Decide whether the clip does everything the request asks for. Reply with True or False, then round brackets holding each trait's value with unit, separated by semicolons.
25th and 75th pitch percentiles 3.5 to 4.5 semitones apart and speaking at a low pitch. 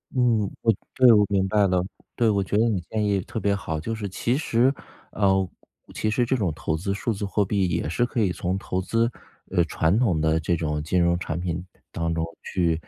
True (4.1 semitones; 95 Hz)